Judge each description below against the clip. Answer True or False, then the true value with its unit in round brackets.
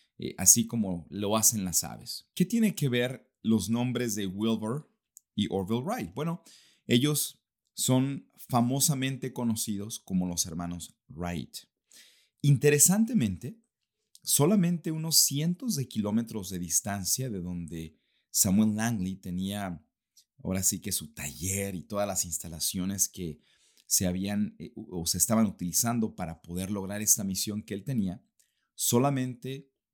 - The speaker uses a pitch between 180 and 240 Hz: False (110 Hz)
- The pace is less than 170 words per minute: True (130 wpm)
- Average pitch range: False (6.0 semitones)